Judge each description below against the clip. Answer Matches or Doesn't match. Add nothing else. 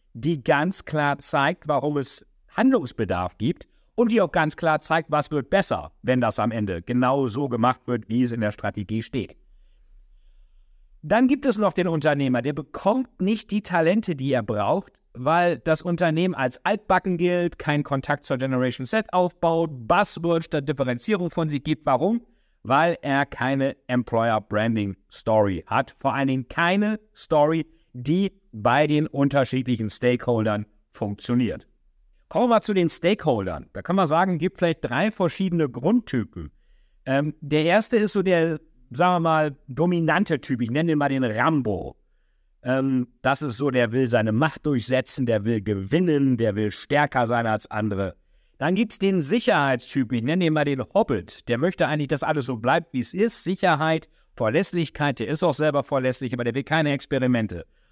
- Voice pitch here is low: Doesn't match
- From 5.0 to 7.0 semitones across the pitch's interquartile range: Matches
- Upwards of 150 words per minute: Matches